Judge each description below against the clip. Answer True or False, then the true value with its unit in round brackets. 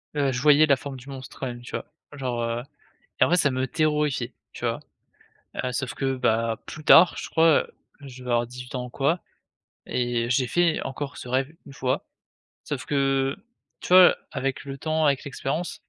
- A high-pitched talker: False (135 Hz)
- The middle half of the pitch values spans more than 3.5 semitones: False (2.8 semitones)